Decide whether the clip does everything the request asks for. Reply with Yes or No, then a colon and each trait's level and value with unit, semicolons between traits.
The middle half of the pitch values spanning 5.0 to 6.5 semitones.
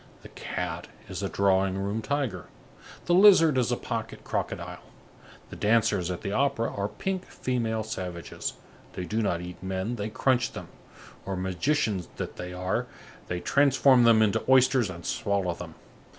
Yes: wide, 5.4 semitones